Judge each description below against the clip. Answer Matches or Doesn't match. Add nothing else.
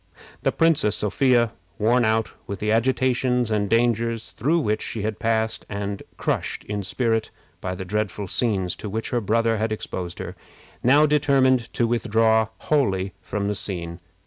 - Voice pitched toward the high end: Doesn't match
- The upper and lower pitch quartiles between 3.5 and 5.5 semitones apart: Doesn't match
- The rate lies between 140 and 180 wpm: Matches